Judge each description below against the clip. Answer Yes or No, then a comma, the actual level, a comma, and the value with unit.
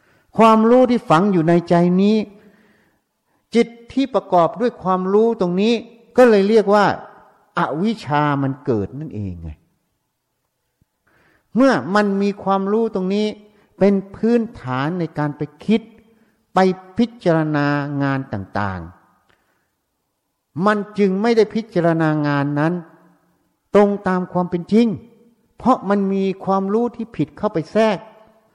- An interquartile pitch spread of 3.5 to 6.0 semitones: Yes, average, 5.3 semitones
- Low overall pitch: No, high, 195 Hz